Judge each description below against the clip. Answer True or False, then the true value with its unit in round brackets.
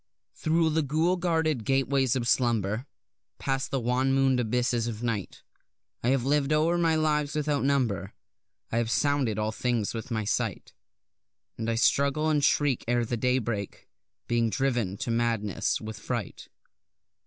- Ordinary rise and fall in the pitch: True (3.8 semitones)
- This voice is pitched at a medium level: False (125 Hz)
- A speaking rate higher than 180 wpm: False (155 wpm)